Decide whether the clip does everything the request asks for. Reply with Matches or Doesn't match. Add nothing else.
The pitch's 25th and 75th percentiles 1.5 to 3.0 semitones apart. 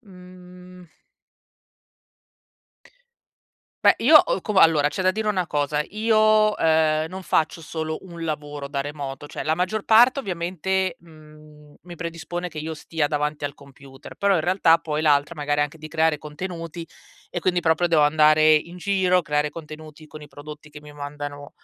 Doesn't match